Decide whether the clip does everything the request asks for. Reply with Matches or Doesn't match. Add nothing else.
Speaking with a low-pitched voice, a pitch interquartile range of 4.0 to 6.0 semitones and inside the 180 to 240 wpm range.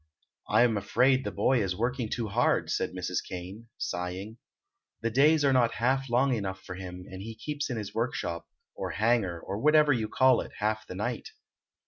Matches